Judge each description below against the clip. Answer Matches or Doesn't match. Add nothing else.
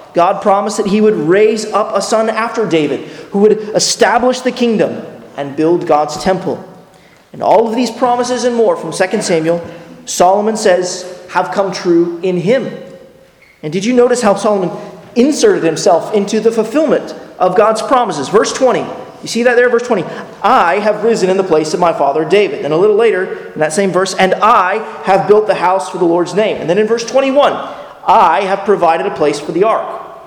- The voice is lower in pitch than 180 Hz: Doesn't match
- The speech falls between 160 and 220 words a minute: Matches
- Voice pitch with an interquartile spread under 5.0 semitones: Matches